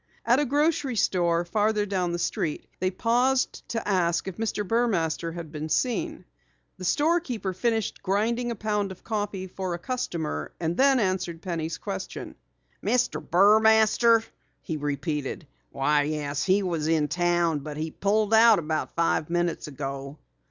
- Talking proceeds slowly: No, average, 155 wpm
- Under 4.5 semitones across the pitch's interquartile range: No, wide, 5.5 semitones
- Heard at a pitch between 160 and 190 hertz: Yes, medium, 185 Hz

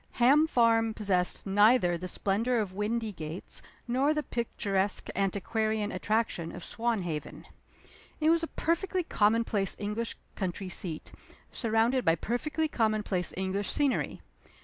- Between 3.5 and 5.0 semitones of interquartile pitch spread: Yes, average, 3.8 semitones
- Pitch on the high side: Yes, high, 215 Hz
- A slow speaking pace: Yes, slow, 120 wpm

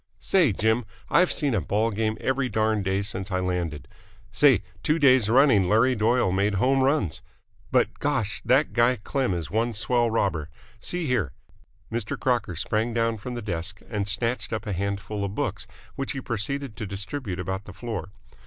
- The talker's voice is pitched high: No, low, 110 Hz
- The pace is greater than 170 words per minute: Yes, average, 180 wpm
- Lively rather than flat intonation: No, average, 4.3 semitones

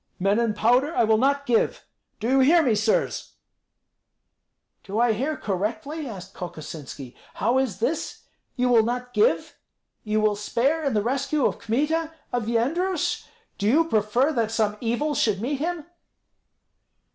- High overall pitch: Yes, high, 240 Hz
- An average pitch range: Yes, average, 4.8 semitones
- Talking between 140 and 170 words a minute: Yes, average, 155 wpm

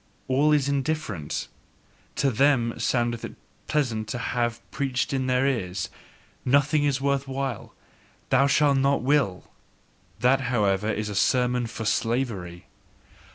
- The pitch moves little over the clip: No, average, 3.6 semitones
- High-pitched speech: No, low, 125 Hz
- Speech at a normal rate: No, slow, 130 wpm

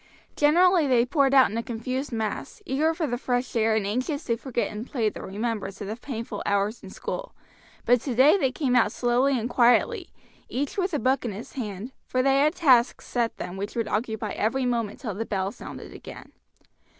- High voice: Yes, high, 245 Hz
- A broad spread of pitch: No, average, 3.7 semitones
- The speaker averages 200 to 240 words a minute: Yes, fast, 205 wpm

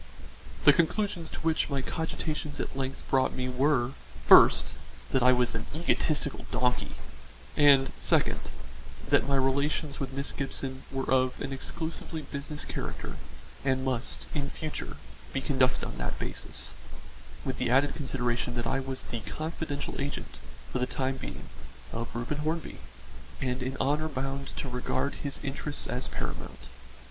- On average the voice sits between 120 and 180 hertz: Yes, low, 135 Hz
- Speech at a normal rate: Yes, average, 150 wpm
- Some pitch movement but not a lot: No, narrow, 2.2 semitones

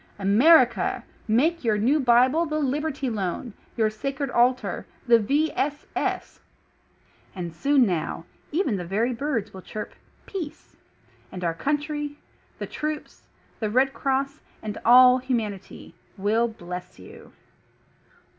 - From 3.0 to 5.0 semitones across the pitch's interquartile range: No, wide, 5.5 semitones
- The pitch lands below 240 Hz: No, very high, 250 Hz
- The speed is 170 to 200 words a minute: No, slow, 135 wpm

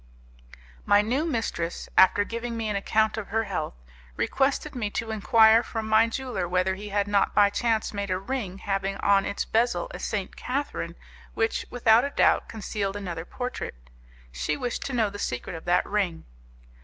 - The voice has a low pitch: No, high, 210 Hz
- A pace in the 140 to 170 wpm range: No, average, 180 wpm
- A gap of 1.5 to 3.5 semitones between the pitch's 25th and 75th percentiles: Yes, average, 2.8 semitones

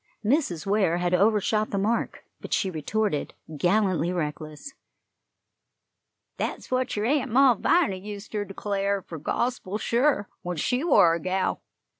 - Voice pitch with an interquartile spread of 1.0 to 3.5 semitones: No, average, 4.6 semitones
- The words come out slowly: Yes, slow, 130 wpm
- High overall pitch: Yes, high, 200 Hz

